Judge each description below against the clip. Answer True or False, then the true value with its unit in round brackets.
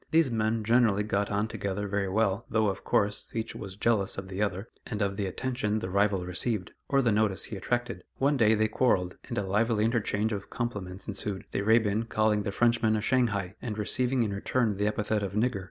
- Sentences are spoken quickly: True (210 wpm)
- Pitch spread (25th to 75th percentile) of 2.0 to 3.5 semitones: True (2.4 semitones)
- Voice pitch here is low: True (105 Hz)